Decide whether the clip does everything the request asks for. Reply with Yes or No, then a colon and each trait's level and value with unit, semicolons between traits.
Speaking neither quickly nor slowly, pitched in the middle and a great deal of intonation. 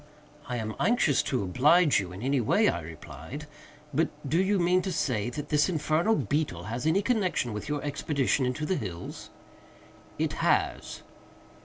Yes: average, 165 wpm; medium, 145 Hz; wide, 7.0 semitones